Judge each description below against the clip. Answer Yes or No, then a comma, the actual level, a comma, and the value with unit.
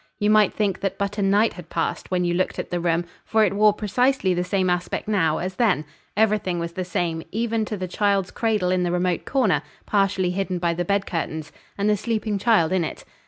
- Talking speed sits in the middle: No, fast, 225 wpm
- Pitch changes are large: No, average, 3.0 semitones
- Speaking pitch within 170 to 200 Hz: Yes, high, 190 Hz